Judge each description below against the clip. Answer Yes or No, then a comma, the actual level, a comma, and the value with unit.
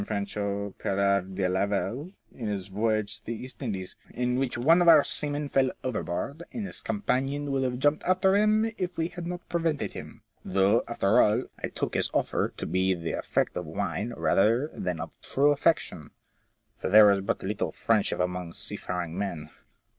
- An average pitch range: No, wide, 6.9 semitones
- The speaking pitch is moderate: No, low, 110 Hz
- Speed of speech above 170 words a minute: Yes, average, 190 wpm